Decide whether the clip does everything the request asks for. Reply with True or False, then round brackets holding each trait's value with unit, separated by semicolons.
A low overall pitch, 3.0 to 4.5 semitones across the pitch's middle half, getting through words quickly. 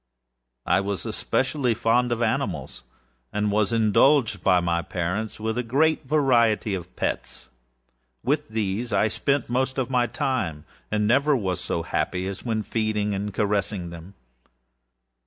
False (110 Hz; 4.1 semitones; 145 wpm)